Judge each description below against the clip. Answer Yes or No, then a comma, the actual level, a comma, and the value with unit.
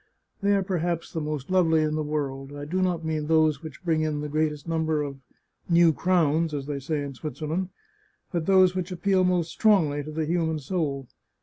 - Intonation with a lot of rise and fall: No, average, 2.9 semitones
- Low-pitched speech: No, medium, 160 Hz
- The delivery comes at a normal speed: No, fast, 210 wpm